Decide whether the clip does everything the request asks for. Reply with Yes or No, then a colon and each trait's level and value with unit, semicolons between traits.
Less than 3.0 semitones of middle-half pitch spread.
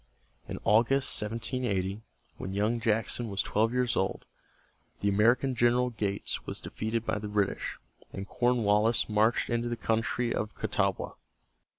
Yes: narrow, 2.5 semitones